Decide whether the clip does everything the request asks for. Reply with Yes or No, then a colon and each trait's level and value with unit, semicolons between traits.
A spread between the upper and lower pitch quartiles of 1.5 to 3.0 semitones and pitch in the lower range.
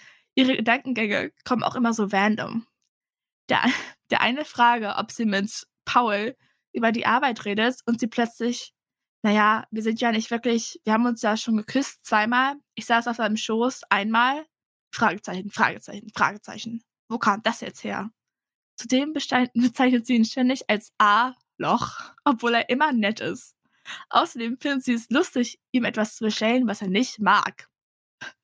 No: narrow, 2.5 semitones; high, 230 Hz